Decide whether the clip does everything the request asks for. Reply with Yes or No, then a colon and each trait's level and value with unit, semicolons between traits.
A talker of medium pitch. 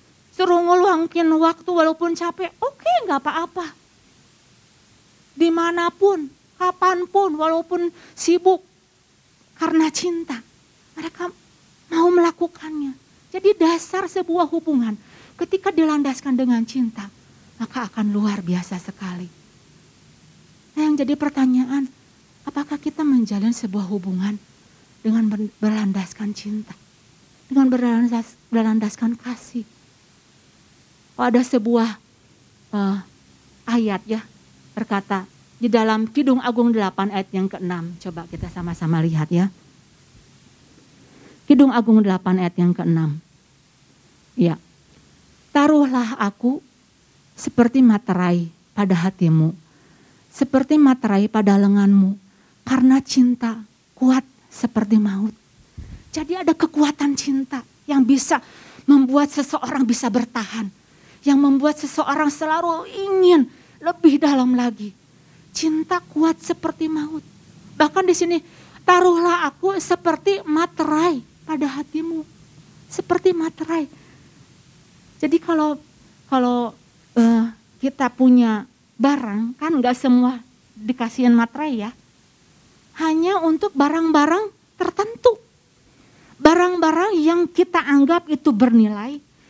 No: very high, 270 Hz